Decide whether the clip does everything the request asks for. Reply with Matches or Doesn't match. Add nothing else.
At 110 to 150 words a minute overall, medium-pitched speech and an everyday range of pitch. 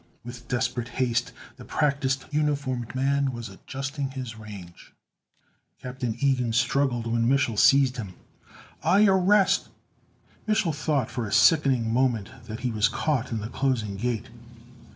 Doesn't match